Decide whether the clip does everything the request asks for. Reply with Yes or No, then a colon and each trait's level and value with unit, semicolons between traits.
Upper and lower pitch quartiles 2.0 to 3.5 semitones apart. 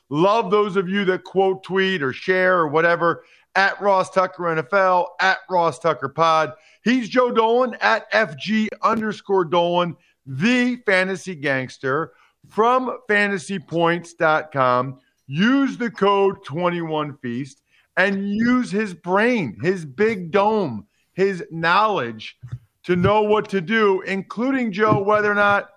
No: average, 4.1 semitones